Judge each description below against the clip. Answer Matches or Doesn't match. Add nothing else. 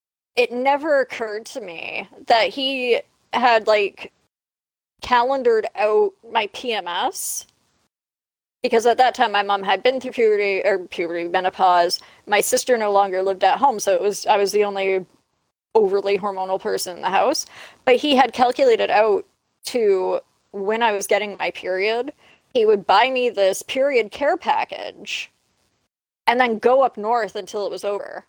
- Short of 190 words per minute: Matches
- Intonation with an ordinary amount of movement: Matches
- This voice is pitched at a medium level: Doesn't match